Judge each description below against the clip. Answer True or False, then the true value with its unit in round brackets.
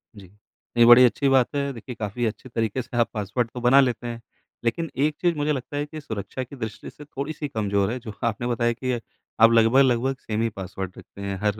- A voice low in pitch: True (120 Hz)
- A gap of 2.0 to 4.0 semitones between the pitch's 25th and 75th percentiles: True (3.4 semitones)